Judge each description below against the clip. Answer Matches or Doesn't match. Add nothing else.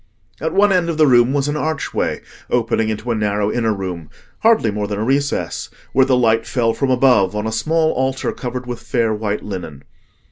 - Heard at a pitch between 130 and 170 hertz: Doesn't match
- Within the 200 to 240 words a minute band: Matches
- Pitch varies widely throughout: Doesn't match